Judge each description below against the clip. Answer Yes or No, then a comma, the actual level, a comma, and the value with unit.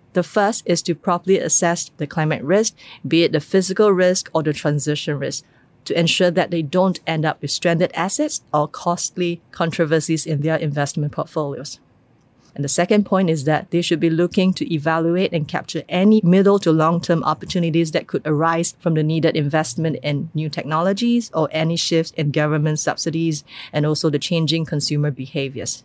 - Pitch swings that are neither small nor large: No, narrow, 2.3 semitones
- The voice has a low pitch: No, medium, 165 Hz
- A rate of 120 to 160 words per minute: No, average, 175 wpm